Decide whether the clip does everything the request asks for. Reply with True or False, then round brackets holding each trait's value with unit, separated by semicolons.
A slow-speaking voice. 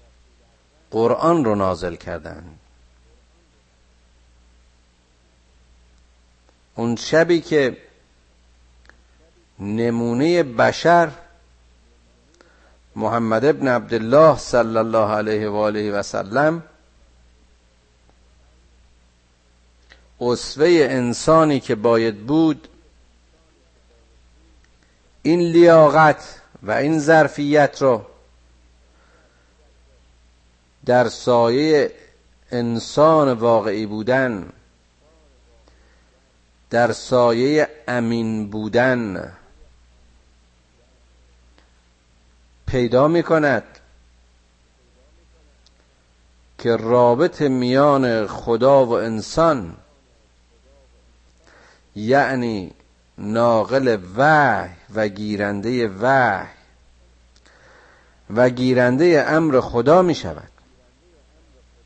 True (55 wpm)